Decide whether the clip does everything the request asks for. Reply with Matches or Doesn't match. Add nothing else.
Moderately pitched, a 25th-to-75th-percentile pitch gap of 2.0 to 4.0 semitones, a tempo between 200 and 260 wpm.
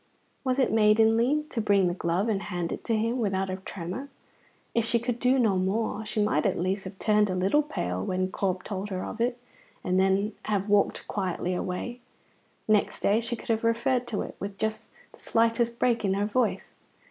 Doesn't match